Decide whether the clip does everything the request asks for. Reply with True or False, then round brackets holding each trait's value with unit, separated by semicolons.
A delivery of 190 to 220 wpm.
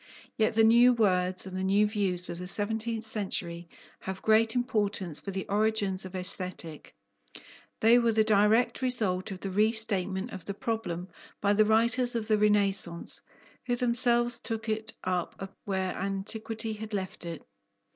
False (155 wpm)